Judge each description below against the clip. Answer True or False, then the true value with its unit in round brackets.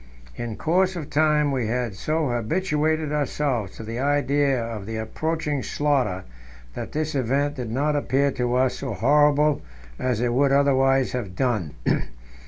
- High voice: False (135 Hz)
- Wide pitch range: False (3.6 semitones)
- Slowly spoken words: False (155 wpm)